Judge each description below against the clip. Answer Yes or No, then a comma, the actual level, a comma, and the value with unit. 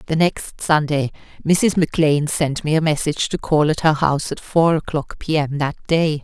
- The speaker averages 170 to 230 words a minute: Yes, average, 200 wpm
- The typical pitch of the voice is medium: Yes, medium, 155 Hz